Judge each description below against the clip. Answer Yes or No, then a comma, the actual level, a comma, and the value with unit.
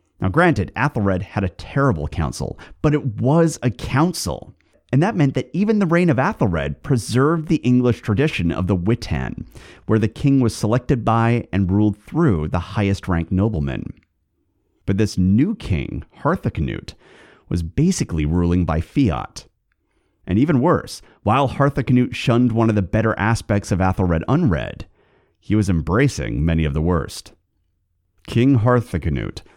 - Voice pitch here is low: Yes, low, 110 Hz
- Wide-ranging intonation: Yes, wide, 6.5 semitones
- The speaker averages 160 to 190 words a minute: No, average, 150 wpm